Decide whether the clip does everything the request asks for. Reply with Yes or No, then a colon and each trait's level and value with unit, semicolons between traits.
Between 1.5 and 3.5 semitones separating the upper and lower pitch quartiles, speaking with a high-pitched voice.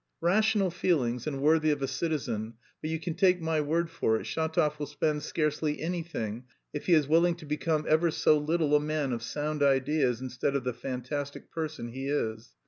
No: average, 3.2 semitones; medium, 150 Hz